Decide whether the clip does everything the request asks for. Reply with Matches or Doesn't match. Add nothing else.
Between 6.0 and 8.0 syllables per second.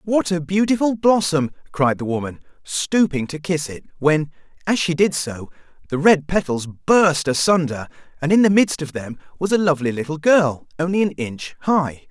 Doesn't match